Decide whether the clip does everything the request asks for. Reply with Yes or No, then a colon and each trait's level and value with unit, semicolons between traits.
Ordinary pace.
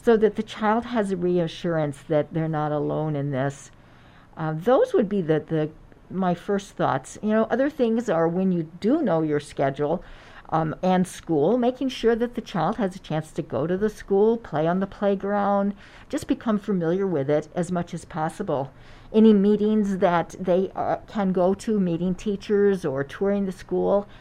Yes: average, 190 wpm